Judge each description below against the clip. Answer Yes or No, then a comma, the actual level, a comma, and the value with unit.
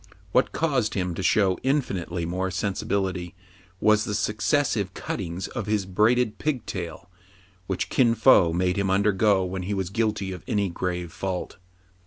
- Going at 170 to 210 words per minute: No, average, 150 wpm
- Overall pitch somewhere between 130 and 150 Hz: No, very low, 95 Hz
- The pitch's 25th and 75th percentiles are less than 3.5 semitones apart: Yes, average, 2.8 semitones